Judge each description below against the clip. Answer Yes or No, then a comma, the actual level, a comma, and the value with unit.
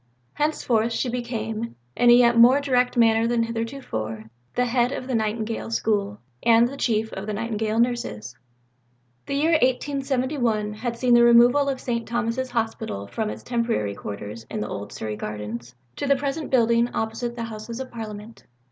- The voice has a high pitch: Yes, high, 230 Hz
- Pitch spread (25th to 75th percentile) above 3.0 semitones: No, narrow, 2.5 semitones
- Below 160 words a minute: No, average, 170 wpm